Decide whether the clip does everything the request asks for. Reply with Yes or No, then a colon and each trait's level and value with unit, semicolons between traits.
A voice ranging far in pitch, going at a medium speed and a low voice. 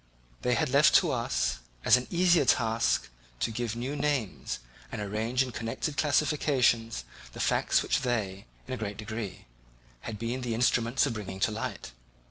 No: average, 3.2 semitones; average, 165 wpm; low, 120 Hz